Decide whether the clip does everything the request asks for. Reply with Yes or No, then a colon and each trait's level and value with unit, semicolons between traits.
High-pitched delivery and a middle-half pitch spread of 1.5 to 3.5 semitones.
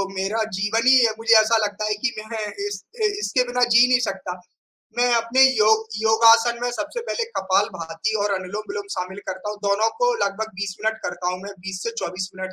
Yes: high, 215 Hz; average, 3.2 semitones